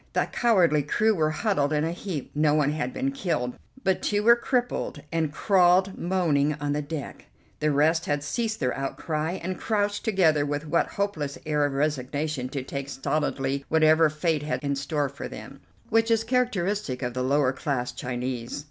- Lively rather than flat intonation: No, average, 4.8 semitones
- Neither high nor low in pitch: Yes, medium, 155 Hz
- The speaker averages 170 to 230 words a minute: Yes, average, 180 wpm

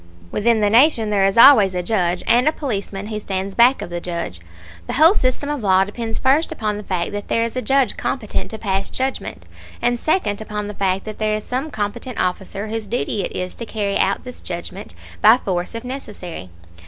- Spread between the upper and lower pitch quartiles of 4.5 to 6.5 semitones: No, average, 3.9 semitones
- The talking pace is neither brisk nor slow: No, fast, 215 wpm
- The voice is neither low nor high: No, high, 210 Hz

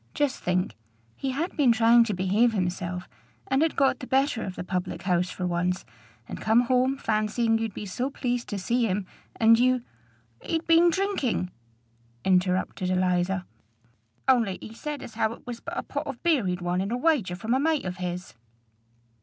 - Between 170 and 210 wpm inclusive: Yes, average, 185 wpm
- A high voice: Yes, high, 225 Hz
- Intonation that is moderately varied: No, wide, 6.1 semitones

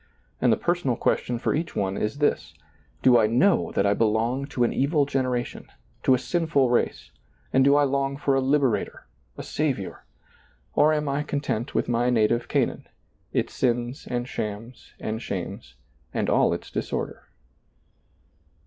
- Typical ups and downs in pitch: Yes, average, 3.4 semitones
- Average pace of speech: Yes, average, 165 wpm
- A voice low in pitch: Yes, low, 130 Hz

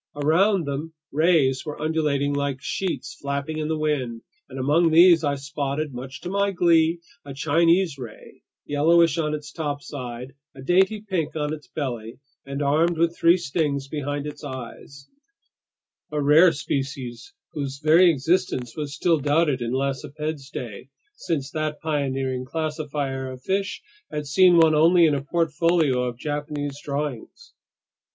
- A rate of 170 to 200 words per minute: No, average, 145 wpm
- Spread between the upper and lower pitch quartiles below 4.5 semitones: Yes, average, 2.9 semitones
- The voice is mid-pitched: Yes, medium, 150 Hz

